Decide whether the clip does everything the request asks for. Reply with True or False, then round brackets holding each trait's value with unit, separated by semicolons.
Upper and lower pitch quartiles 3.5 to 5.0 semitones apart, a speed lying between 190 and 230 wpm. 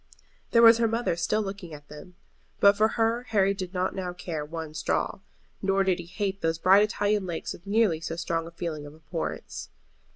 True (3.8 semitones; 200 wpm)